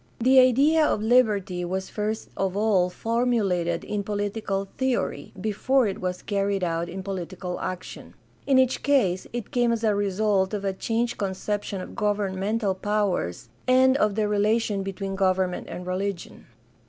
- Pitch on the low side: No, high, 205 Hz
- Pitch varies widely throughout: No, average, 3.1 semitones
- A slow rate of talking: No, average, 155 wpm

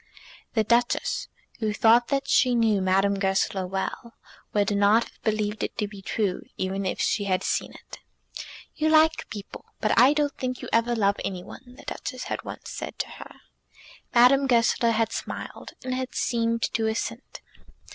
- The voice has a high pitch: Yes, high, 225 Hz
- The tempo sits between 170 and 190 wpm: Yes, average, 175 wpm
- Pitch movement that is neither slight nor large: Yes, average, 3.6 semitones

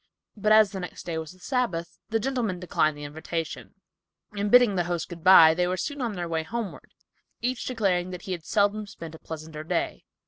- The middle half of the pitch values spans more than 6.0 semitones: No, average, 4.5 semitones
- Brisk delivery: Yes, fast, 210 wpm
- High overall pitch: No, medium, 180 Hz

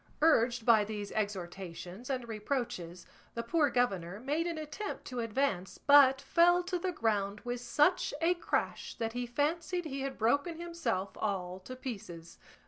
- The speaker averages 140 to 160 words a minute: Yes, average, 155 wpm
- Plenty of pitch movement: Yes, wide, 6.5 semitones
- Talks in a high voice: Yes, high, 245 Hz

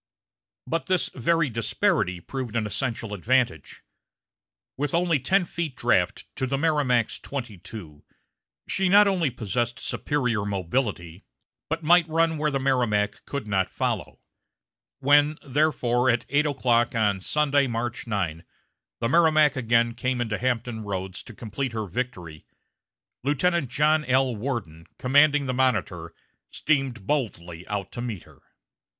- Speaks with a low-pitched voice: Yes, low, 125 Hz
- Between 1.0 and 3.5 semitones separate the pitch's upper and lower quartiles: No, wide, 5.6 semitones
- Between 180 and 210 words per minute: No, slow, 135 wpm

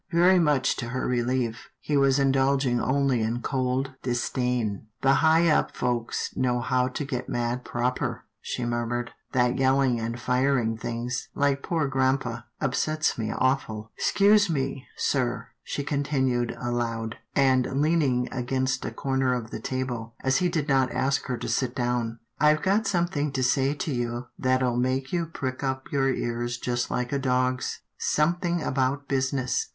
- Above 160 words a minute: Yes, average, 170 wpm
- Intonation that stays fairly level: Yes, narrow, 2.3 semitones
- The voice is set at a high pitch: No, low, 130 Hz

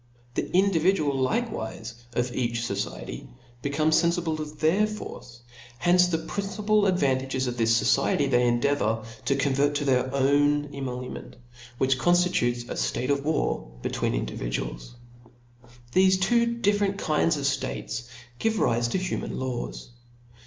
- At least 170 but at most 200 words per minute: No, slow, 135 wpm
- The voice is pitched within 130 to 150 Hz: Yes, medium, 140 Hz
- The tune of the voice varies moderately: No, wide, 6.6 semitones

